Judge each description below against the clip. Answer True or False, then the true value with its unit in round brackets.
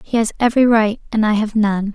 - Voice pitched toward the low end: False (220 Hz)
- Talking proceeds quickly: True (245 wpm)